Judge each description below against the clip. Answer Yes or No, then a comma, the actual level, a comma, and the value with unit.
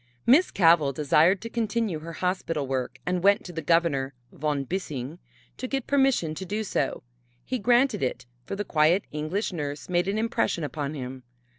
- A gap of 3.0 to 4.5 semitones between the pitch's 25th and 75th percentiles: No, wide, 5.6 semitones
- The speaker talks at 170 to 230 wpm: Yes, average, 175 wpm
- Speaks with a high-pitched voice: No, medium, 170 Hz